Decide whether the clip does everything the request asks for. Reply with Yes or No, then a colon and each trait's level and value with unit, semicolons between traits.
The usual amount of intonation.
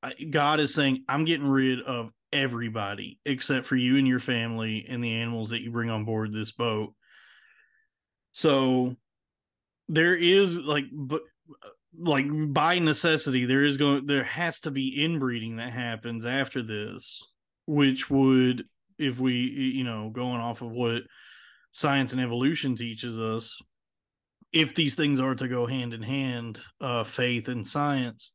Yes: average, 3.6 semitones